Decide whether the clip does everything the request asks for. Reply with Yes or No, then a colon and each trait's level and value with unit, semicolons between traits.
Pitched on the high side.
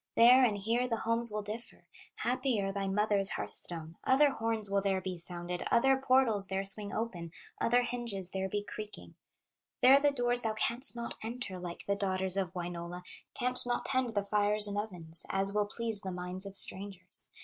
Yes: high, 205 Hz